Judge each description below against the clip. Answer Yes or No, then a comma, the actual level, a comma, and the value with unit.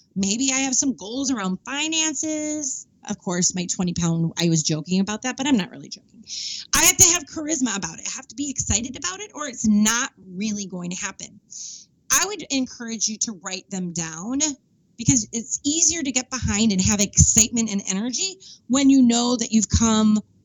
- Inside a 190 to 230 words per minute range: Yes, average, 200 wpm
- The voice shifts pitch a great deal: Yes, wide, 5.7 semitones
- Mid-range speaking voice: No, high, 230 Hz